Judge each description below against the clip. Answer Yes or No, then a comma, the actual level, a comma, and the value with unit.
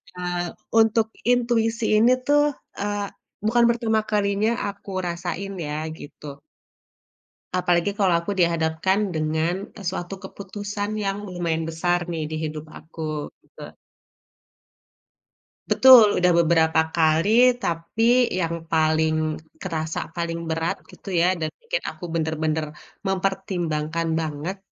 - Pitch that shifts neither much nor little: Yes, average, 4.1 semitones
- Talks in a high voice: No, medium, 175 Hz